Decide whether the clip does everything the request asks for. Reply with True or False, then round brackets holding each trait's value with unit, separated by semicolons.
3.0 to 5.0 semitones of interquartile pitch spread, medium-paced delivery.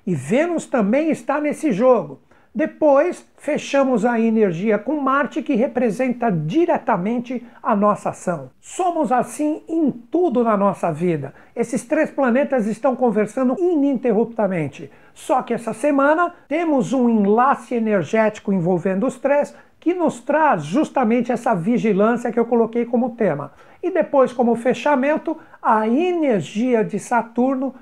True (4.4 semitones; 130 wpm)